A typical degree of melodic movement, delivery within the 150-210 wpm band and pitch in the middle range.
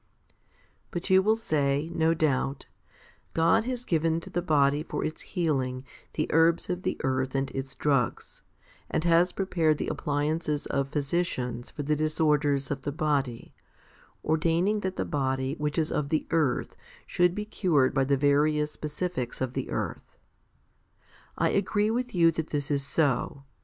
Yes: average, 3.4 semitones; average, 160 wpm; medium, 150 Hz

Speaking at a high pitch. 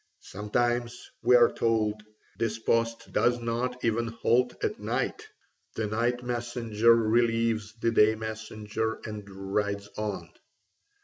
No: low, 115 Hz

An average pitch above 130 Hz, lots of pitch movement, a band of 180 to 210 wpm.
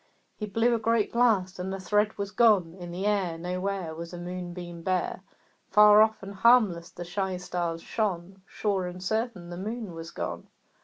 No: high, 190 Hz; average, 3.1 semitones; average, 185 wpm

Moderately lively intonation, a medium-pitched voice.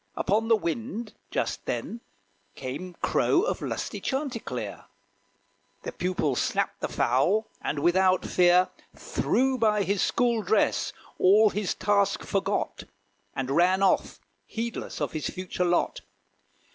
No: average, 3.9 semitones; high, 195 Hz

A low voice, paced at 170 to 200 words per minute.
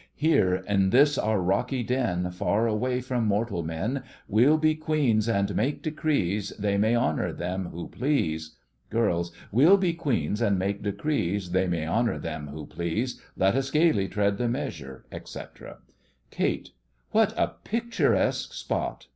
No: low, 105 Hz; average, 150 wpm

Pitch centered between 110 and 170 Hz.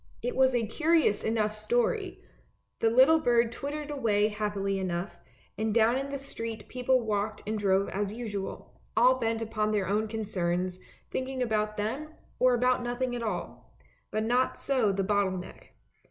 No: high, 225 Hz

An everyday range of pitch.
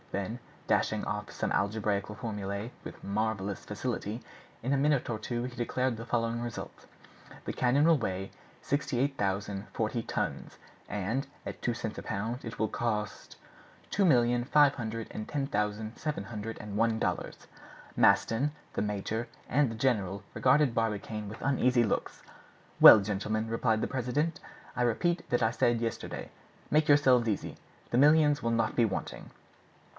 Yes: average, 3.3 semitones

